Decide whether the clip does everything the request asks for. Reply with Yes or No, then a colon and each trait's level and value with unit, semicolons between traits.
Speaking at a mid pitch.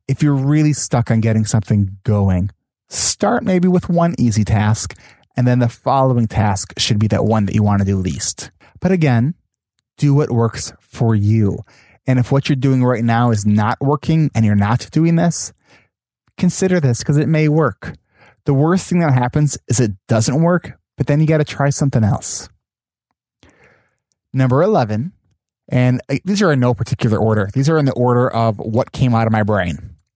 No: low, 125 Hz